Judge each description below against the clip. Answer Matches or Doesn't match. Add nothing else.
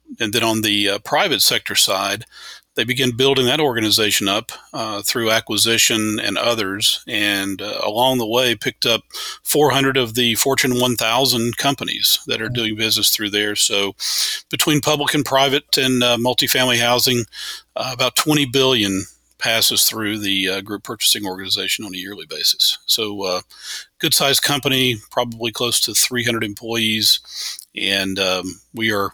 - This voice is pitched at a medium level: Doesn't match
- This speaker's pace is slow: Doesn't match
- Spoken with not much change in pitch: Doesn't match